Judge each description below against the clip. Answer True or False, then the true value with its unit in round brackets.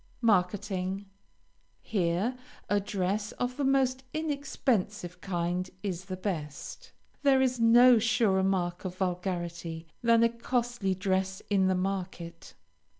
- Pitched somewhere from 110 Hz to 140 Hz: False (195 Hz)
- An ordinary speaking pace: False (120 wpm)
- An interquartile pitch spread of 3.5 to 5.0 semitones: True (4.5 semitones)